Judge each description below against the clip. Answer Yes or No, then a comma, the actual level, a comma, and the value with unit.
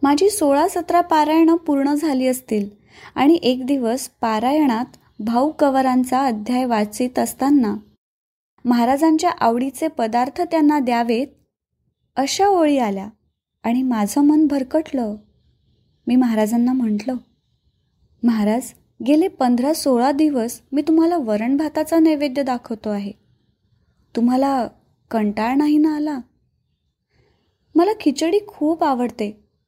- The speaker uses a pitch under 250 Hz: No, very high, 265 Hz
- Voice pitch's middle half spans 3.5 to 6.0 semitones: Yes, average, 4.4 semitones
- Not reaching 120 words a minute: Yes, average, 105 wpm